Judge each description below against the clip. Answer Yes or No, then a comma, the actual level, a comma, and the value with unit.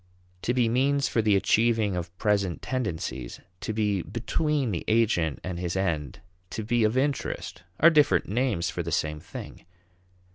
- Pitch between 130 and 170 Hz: No, low, 105 Hz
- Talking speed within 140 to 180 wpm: Yes, average, 160 wpm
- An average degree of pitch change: No, wide, 5.8 semitones